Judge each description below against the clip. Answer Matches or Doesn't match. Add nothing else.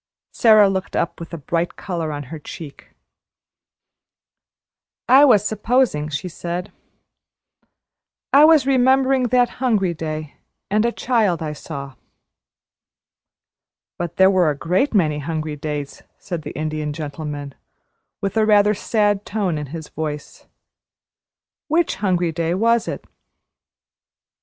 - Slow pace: Matches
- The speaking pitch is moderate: Matches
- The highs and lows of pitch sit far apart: Matches